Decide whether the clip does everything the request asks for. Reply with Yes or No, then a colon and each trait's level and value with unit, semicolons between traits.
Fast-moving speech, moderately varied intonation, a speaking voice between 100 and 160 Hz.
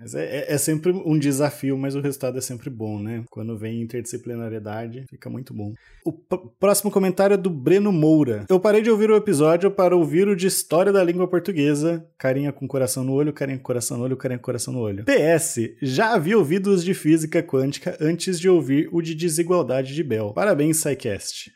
No: fast, 205 wpm; wide, 5.9 semitones; medium, 150 Hz